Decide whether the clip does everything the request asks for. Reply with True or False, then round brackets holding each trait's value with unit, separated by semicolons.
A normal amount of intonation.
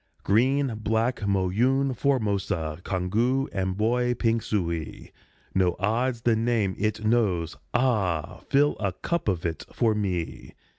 True (4.6 semitones)